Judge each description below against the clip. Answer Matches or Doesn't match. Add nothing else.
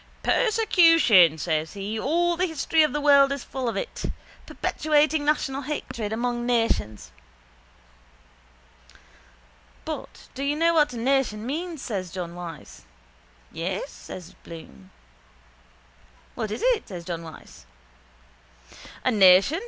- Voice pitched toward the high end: Matches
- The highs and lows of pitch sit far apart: Matches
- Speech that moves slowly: Matches